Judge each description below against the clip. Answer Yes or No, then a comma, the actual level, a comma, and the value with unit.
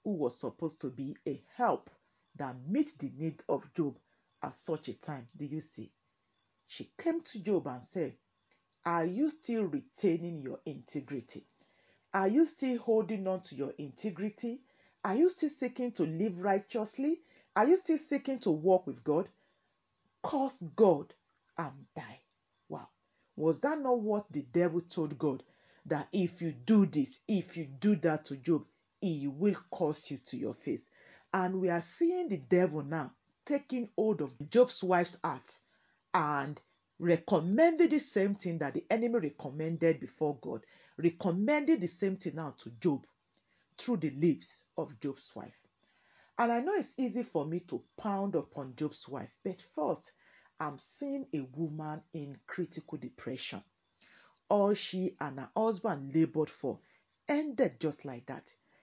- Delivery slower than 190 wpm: Yes, average, 160 wpm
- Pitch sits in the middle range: Yes, medium, 175 Hz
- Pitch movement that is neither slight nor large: No, wide, 7.0 semitones